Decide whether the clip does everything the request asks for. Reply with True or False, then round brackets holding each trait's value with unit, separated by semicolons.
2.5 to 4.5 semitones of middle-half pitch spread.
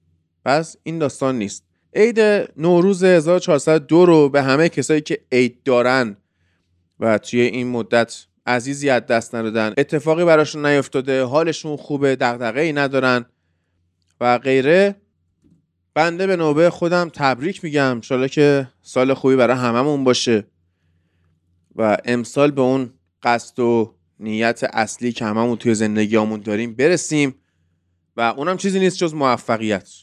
False (5.3 semitones)